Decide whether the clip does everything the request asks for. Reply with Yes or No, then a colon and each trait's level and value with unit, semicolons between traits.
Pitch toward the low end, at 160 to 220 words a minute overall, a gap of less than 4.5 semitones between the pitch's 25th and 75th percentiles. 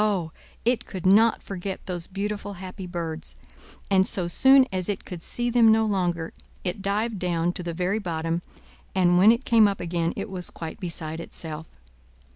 No: medium, 185 Hz; average, 180 wpm; average, 3.3 semitones